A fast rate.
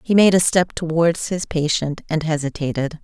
No: average, 180 wpm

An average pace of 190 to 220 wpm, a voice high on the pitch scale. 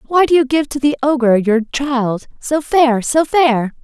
Yes: fast, 205 wpm; very high, 270 Hz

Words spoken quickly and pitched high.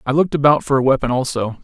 No: fast, 260 wpm; low, 135 Hz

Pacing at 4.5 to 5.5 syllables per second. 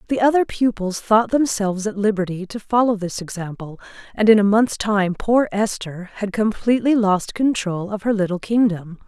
Yes: 5.0 syllables/s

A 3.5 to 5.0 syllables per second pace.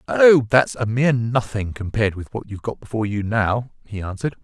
No: 6.0 syllables/s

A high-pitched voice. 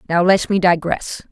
No: medium, 180 Hz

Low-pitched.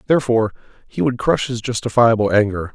Yes: low, 115 Hz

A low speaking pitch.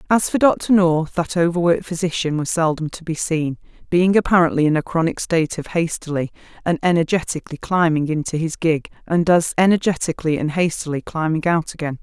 No: medium, 165 Hz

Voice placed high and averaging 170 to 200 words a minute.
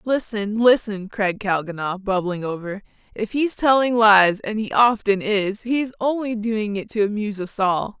No: high, 210 Hz; average, 150 wpm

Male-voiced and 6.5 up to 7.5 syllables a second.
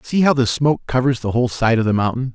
Yes: male; 6.8 syllables/s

